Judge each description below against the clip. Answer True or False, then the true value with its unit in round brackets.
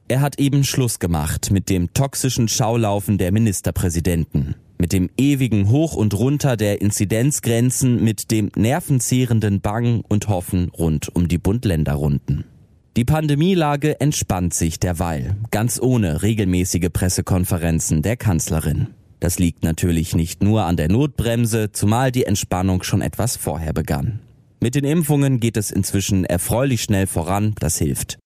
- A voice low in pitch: True (105 Hz)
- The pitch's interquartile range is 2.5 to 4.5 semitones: False (5.2 semitones)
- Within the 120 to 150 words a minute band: True (140 wpm)